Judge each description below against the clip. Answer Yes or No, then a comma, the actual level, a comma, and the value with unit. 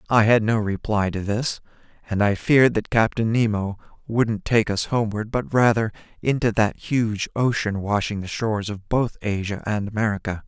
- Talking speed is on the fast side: No, average, 170 wpm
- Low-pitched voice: Yes, low, 110 Hz